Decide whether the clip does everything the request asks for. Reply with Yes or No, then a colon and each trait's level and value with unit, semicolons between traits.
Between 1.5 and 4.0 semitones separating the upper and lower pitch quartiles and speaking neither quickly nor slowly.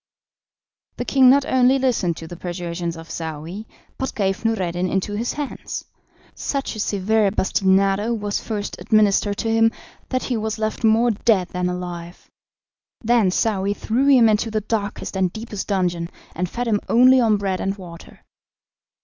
Yes: average, 3.7 semitones; average, 160 wpm